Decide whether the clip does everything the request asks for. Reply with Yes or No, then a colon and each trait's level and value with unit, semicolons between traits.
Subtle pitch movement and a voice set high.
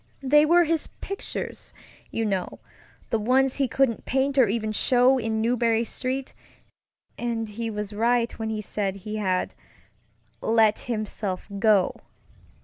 No: average, 3.3 semitones; high, 225 Hz